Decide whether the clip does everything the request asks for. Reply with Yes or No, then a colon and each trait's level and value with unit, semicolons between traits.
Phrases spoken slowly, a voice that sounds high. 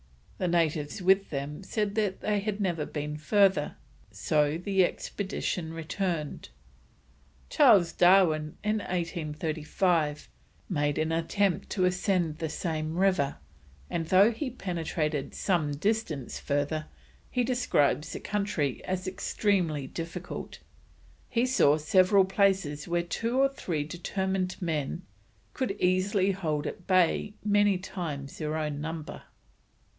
No: slow, 120 wpm; medium, 175 Hz